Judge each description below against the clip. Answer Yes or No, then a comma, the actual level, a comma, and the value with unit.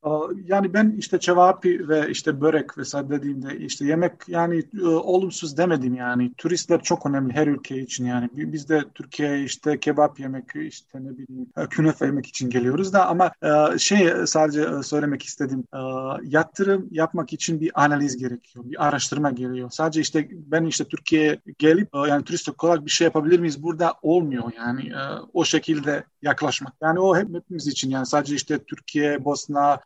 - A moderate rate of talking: No, fast, 160 wpm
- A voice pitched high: No, medium, 150 Hz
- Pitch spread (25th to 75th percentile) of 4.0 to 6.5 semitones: No, average, 3.4 semitones